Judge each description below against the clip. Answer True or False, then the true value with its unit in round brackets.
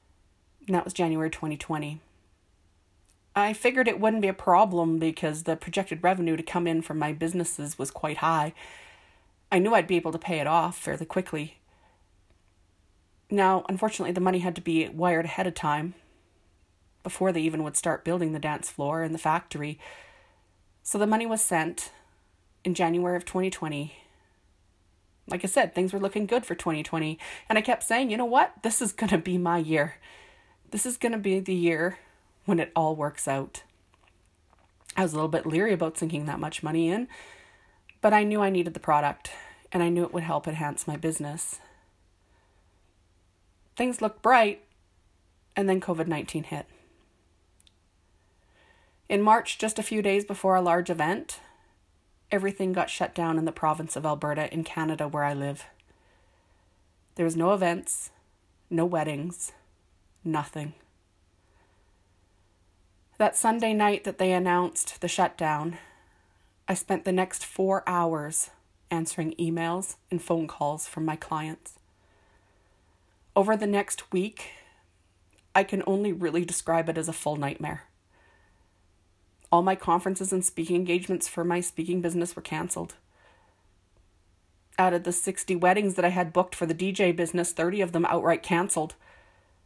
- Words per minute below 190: True (160 wpm)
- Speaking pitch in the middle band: True (165 Hz)